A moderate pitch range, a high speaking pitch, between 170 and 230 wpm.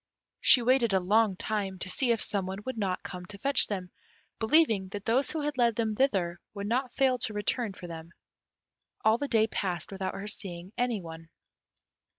Yes: average, 4.3 semitones; high, 210 Hz; average, 195 wpm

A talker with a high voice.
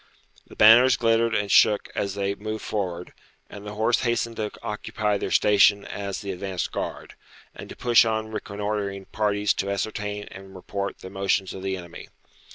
No: low, 105 Hz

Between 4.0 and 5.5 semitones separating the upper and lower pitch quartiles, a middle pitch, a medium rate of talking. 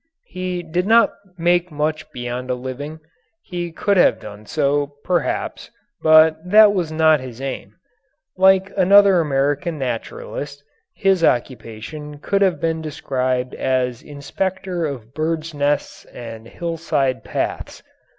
No: average, 5.0 semitones; medium, 155 Hz; slow, 125 wpm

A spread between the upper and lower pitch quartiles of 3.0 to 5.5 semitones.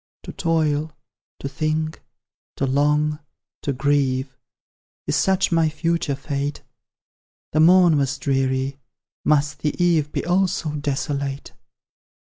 No: narrow, 2.4 semitones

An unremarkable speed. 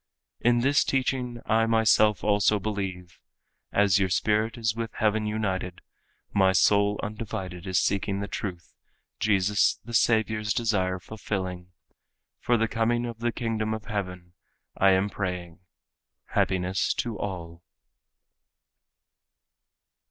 No: slow, 115 wpm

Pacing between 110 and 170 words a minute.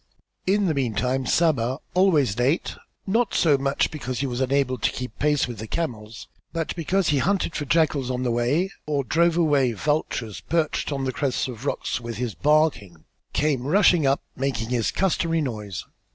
No: average, 180 wpm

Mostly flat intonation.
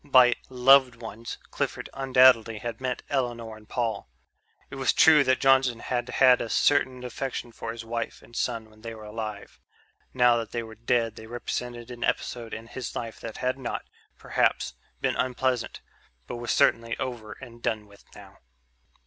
Yes: narrow, 2.0 semitones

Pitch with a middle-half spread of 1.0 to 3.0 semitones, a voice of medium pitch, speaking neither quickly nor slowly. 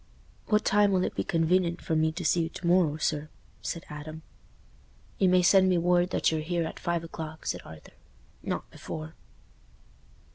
Yes: narrow, 2.4 semitones; medium, 170 Hz; average, 180 wpm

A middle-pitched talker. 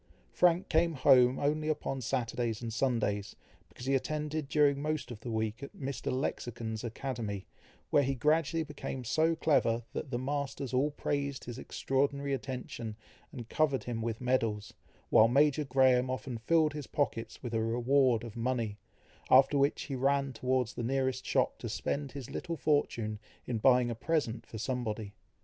No: low, 130 Hz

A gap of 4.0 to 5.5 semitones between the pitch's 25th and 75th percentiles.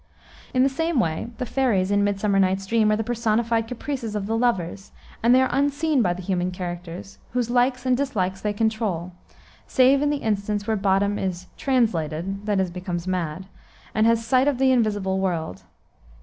Yes: average, 4.8 semitones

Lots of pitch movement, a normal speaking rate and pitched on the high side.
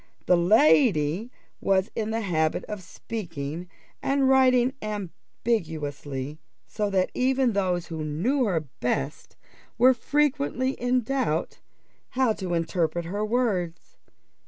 No: wide, 7.0 semitones; slow, 115 wpm; high, 205 Hz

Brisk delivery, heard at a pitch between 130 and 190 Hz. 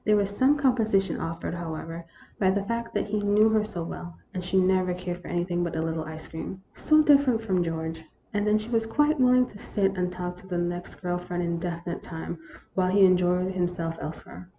Yes: fast, 220 wpm; medium, 185 Hz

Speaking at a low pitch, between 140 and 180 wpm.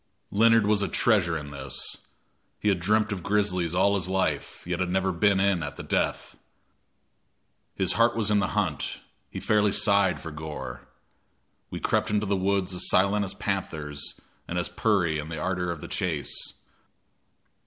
Yes: very low, 95 Hz; average, 175 wpm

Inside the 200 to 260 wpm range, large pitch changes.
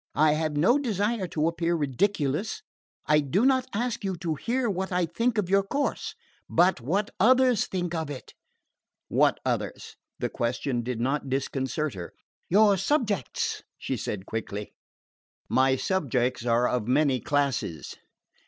No: average, 145 wpm; wide, 7.4 semitones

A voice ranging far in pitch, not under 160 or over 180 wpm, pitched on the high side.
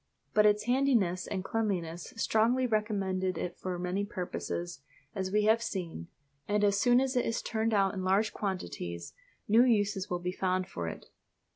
No: average, 3.2 semitones; average, 170 wpm; high, 200 Hz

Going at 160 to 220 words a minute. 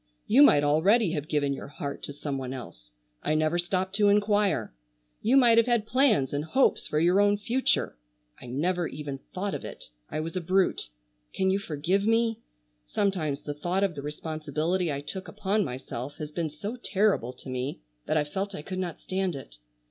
Yes: average, 195 wpm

